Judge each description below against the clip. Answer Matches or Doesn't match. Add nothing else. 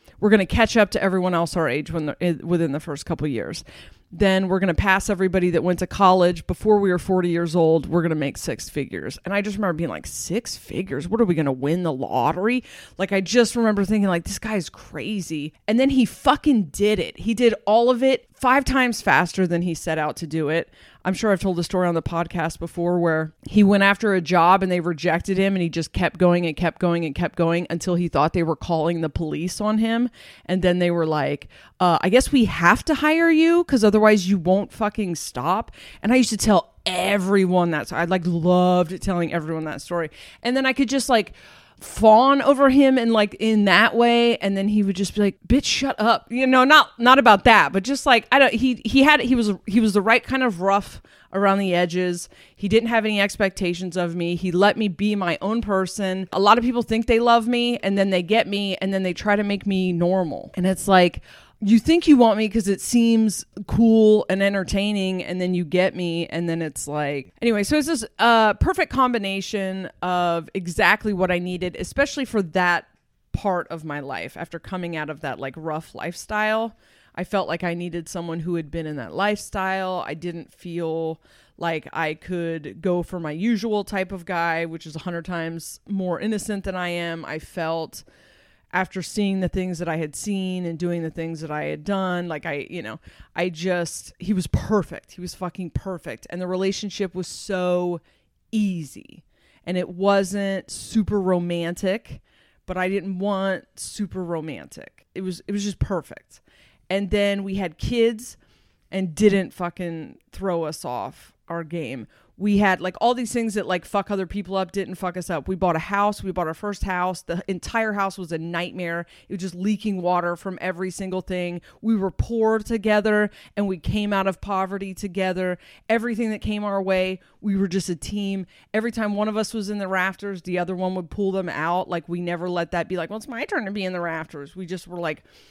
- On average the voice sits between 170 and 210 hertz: Matches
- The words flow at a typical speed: Doesn't match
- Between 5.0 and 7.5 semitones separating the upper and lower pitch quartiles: Doesn't match